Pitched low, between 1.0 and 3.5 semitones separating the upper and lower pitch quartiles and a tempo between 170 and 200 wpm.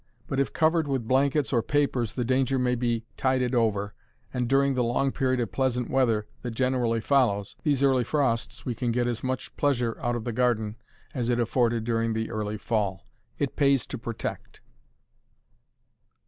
Yes: low, 125 Hz; narrow, 2.6 semitones; average, 175 wpm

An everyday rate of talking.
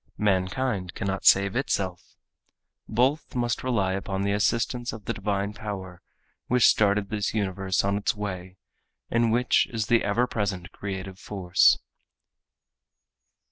No: slow, 130 wpm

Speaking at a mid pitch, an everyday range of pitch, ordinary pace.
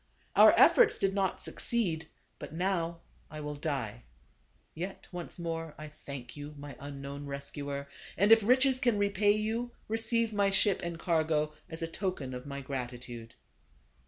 No: medium, 165 Hz; wide, 6.1 semitones; average, 160 wpm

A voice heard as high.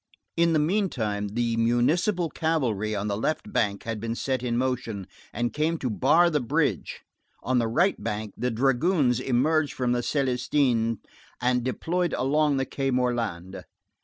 No: low, 125 Hz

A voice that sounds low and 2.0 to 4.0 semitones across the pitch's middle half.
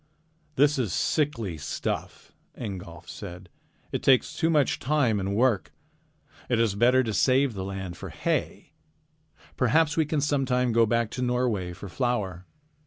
No: low, 120 Hz; wide, 5.5 semitones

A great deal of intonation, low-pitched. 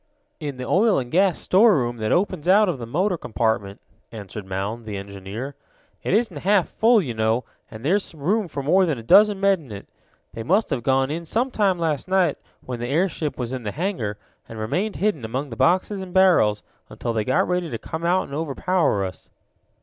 No: wide, 8.5 semitones; medium, 150 Hz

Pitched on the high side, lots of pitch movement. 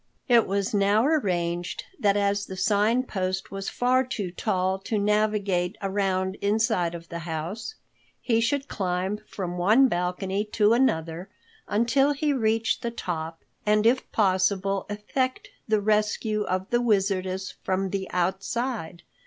No: high, 200 Hz; average, 3.1 semitones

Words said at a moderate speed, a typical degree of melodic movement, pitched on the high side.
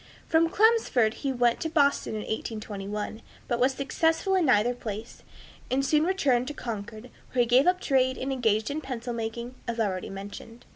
Yes: average, 180 wpm; average, 4.2 semitones; high, 245 Hz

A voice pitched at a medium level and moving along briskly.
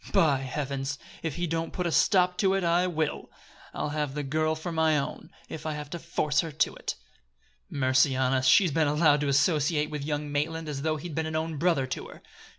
Yes: medium, 155 Hz; fast, 225 wpm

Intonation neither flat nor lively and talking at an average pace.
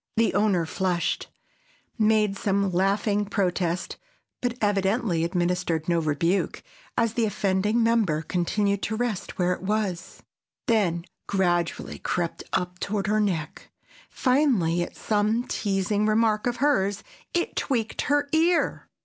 No: average, 3.6 semitones; slow, 125 wpm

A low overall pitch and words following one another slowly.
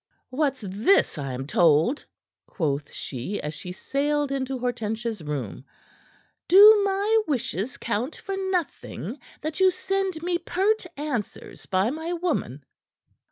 No: very high, 270 Hz; slow, 125 wpm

